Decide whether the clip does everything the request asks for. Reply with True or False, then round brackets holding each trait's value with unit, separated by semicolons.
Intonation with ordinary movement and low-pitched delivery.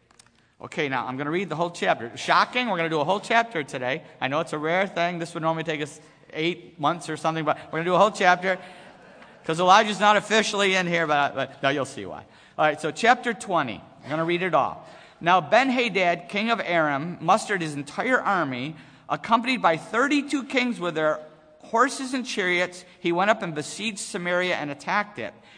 False (5.0 semitones; 175 Hz)